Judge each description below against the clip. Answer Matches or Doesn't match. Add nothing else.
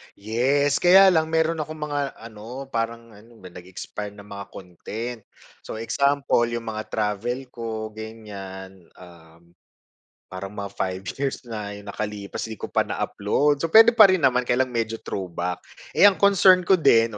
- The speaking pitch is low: Matches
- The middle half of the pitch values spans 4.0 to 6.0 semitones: Matches